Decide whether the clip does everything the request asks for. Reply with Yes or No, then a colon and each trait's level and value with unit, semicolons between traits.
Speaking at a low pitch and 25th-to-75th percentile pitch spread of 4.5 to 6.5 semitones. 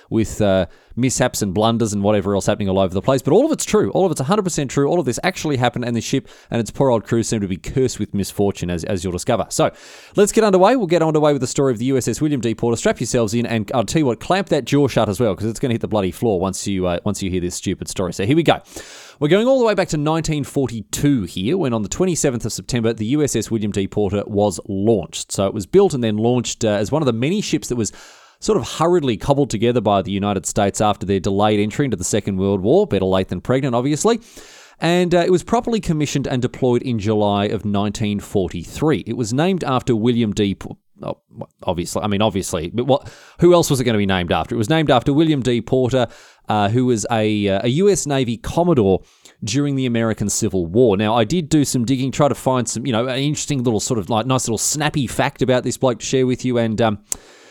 Yes: low, 120 Hz; wide, 5.6 semitones